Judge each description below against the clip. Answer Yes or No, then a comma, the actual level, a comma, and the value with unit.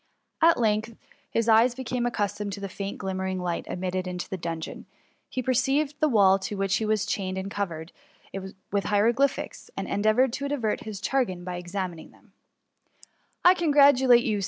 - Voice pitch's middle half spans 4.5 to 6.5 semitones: Yes, average, 5.0 semitones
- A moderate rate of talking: Yes, average, 175 wpm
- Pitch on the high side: Yes, high, 210 Hz